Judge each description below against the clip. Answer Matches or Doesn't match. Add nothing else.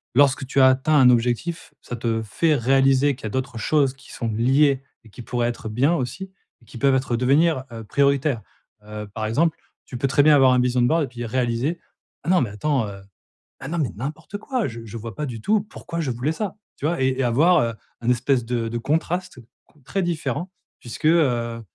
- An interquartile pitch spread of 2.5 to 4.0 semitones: Doesn't match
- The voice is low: Matches